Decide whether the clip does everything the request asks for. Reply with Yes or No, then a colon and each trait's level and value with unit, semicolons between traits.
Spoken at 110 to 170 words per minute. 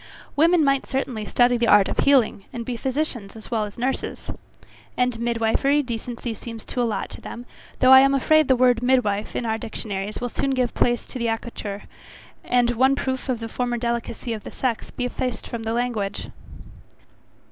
No: average, 185 wpm